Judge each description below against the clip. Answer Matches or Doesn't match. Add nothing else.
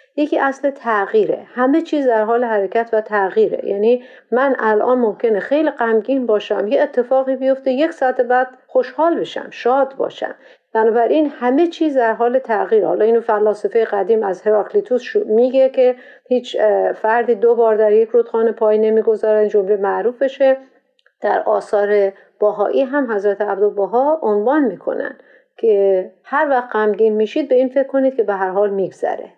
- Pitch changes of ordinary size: Matches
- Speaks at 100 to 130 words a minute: Doesn't match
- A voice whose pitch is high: Matches